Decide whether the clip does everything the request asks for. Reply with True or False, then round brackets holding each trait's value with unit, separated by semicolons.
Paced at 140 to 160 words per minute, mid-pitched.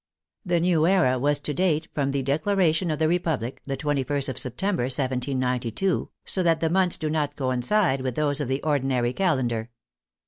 False (180 wpm; 145 Hz)